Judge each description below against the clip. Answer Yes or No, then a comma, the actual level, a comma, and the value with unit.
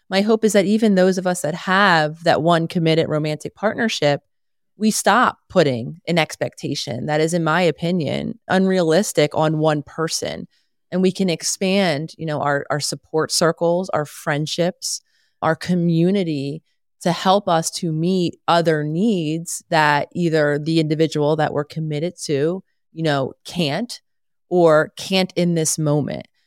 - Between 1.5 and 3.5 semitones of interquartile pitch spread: Yes, average, 3.0 semitones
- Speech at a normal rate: Yes, average, 150 wpm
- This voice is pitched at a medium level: Yes, medium, 165 Hz